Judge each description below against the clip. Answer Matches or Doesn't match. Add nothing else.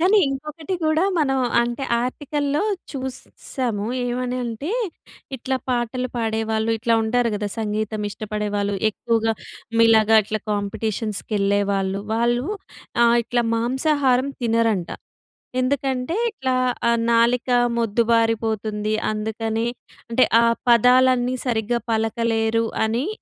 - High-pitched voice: Matches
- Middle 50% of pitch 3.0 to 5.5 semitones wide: Doesn't match